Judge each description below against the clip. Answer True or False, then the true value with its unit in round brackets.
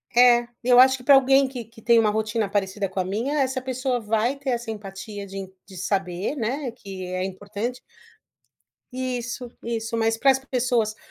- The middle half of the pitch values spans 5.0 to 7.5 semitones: False (3.9 semitones)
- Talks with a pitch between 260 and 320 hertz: False (230 Hz)